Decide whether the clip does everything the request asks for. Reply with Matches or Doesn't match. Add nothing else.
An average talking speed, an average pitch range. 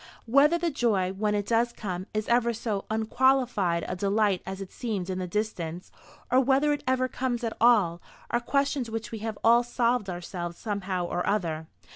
Matches